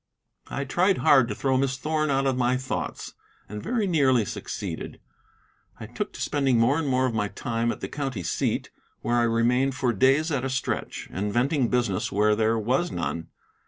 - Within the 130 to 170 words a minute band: No, average, 190 wpm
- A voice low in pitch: Yes, low, 130 Hz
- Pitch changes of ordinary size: Yes, average, 3.1 semitones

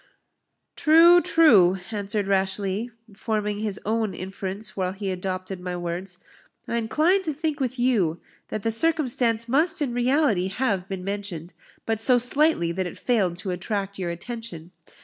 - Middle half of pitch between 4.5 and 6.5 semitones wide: Yes, average, 4.8 semitones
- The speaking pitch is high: Yes, high, 210 Hz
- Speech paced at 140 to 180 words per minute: Yes, average, 150 wpm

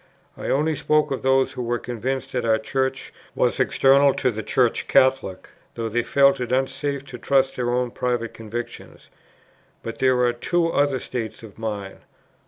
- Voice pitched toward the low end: Yes, low, 125 Hz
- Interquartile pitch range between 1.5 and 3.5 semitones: Yes, narrow, 2.5 semitones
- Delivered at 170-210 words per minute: Yes, average, 180 wpm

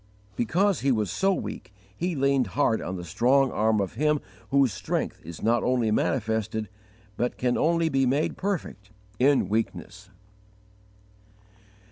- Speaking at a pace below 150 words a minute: Yes, average, 140 wpm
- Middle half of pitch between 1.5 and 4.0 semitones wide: No, average, 4.6 semitones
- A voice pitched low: Yes, low, 125 Hz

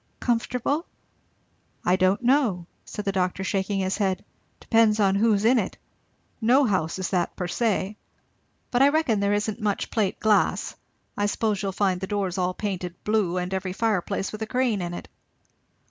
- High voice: Yes, high, 200 Hz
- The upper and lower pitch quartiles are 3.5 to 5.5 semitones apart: No, average, 3.0 semitones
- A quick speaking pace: No, average, 175 wpm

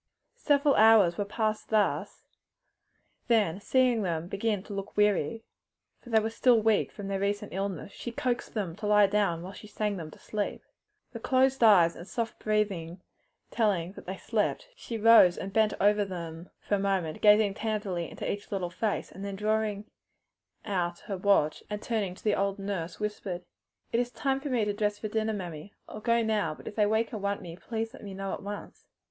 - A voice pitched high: Yes, high, 205 Hz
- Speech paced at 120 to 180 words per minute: No, average, 195 wpm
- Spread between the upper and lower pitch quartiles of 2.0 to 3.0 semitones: Yes, narrow, 2.4 semitones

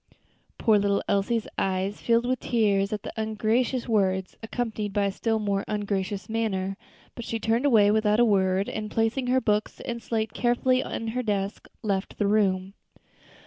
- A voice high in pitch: Yes, high, 215 Hz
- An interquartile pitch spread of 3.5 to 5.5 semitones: No, narrow, 2.4 semitones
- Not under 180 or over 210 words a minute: No, average, 170 wpm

